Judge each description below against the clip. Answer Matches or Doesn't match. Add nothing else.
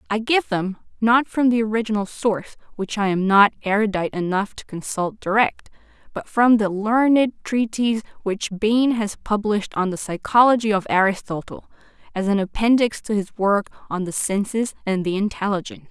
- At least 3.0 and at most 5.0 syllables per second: Doesn't match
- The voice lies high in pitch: Matches